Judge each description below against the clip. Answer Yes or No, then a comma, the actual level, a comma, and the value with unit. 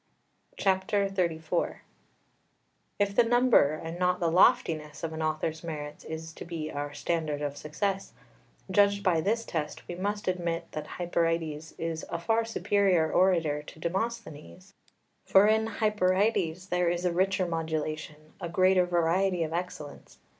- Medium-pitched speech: Yes, medium, 170 Hz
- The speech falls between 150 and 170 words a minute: No, average, 140 wpm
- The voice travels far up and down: No, average, 3.3 semitones